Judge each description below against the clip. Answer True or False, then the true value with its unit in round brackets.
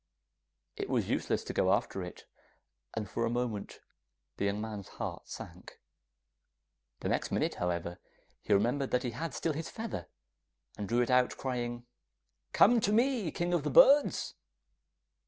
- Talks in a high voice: False (120 Hz)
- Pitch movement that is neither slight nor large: False (7.9 semitones)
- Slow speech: False (155 wpm)